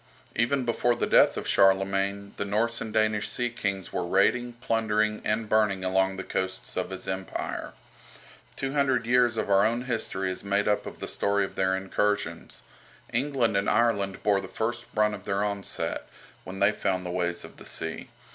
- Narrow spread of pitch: No, average, 3.3 semitones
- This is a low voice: Yes, low, 105 Hz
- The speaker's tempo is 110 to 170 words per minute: No, average, 185 wpm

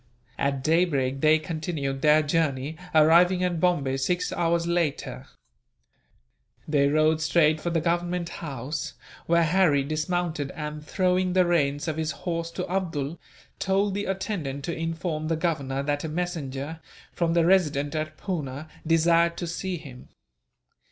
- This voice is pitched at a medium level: Yes, medium, 160 Hz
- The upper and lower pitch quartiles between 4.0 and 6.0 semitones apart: No, average, 3.1 semitones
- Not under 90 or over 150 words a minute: Yes, average, 145 wpm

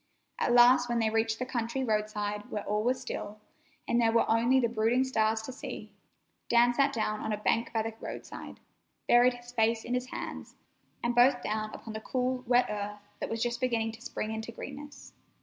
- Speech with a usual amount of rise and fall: No, narrow, 2.2 semitones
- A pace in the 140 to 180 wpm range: No, average, 200 wpm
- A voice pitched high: Yes, high, 235 Hz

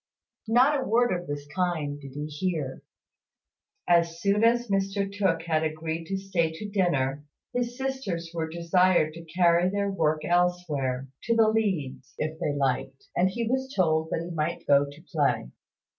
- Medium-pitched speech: Yes, medium, 170 Hz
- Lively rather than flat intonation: No, average, 4.3 semitones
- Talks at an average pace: Yes, average, 170 wpm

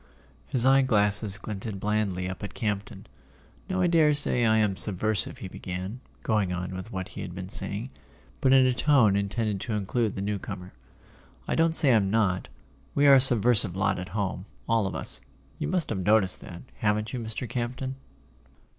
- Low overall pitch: Yes, low, 105 Hz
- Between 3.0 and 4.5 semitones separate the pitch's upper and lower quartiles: Yes, average, 4.2 semitones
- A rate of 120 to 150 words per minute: No, average, 180 wpm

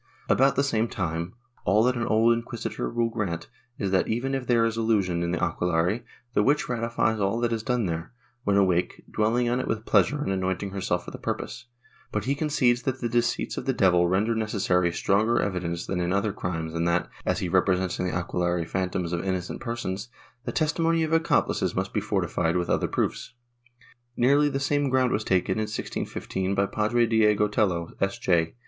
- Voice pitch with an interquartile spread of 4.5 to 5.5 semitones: Yes, average, 4.8 semitones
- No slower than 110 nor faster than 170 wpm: No, average, 200 wpm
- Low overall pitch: Yes, low, 105 Hz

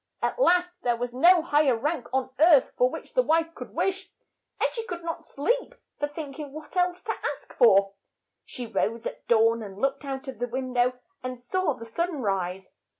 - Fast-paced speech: Yes, fast, 210 wpm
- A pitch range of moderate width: No, wide, 6.0 semitones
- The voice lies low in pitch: No, very high, 275 Hz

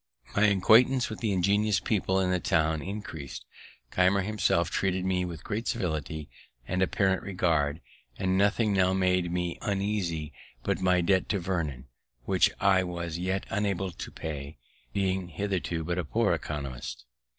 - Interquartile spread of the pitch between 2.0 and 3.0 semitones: Yes, average, 2.7 semitones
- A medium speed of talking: Yes, average, 150 wpm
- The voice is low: Yes, very low, 95 Hz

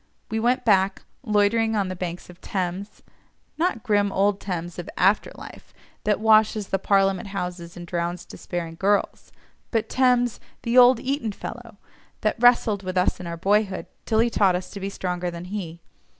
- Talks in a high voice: Yes, high, 200 Hz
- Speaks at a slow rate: No, average, 165 wpm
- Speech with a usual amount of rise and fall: Yes, average, 3.6 semitones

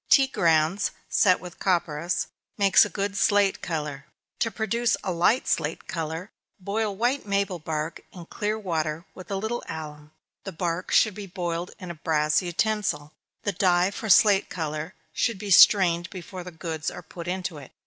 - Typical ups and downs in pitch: Yes, average, 3.8 semitones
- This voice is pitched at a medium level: Yes, medium, 180 Hz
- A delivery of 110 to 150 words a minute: No, average, 170 wpm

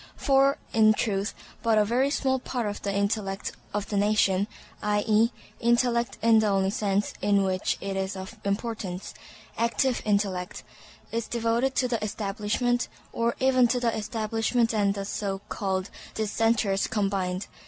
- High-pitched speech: Yes, high, 215 Hz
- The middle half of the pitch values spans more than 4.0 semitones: No, average, 2.8 semitones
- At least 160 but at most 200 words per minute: No, average, 145 wpm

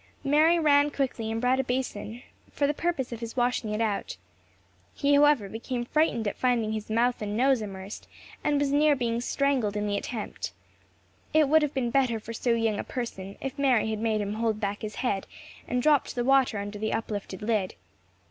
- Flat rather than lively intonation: No, average, 4.3 semitones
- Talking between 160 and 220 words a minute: Yes, average, 200 wpm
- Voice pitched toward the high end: Yes, high, 240 Hz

